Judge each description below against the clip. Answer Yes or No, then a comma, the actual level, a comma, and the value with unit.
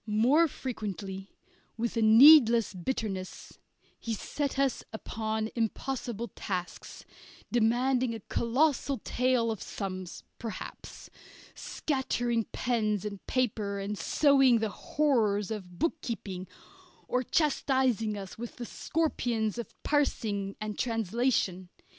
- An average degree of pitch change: Yes, average, 3.7 semitones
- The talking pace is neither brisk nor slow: No, slow, 105 wpm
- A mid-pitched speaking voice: No, high, 230 Hz